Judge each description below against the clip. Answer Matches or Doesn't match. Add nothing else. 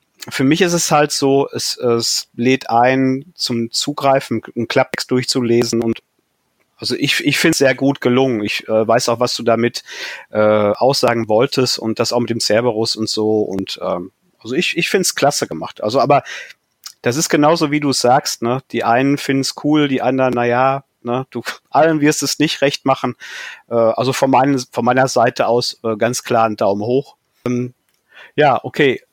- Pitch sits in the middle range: Doesn't match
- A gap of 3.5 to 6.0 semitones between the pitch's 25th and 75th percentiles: Doesn't match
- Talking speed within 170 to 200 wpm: Matches